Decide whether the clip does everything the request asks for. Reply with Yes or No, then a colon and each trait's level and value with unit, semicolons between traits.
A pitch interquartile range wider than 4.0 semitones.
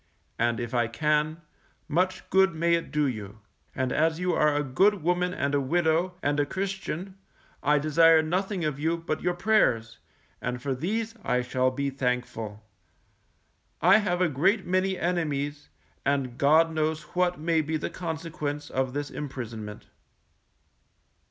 Yes: average, 4.9 semitones